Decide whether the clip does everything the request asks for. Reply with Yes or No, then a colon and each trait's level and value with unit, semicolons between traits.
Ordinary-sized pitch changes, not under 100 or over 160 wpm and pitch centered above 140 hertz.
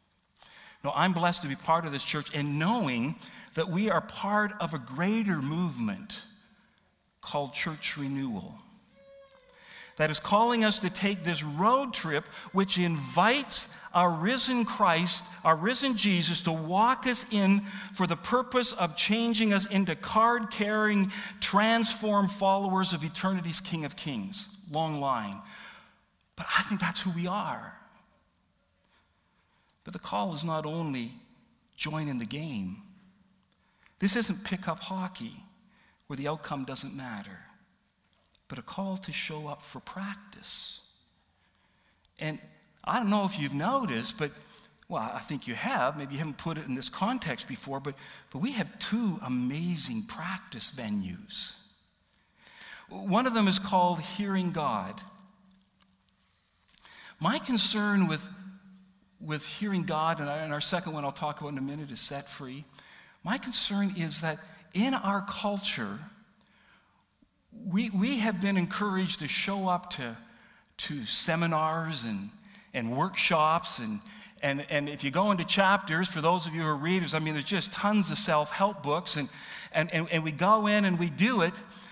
Yes: average, 5.0 semitones; average, 150 wpm; medium, 185 Hz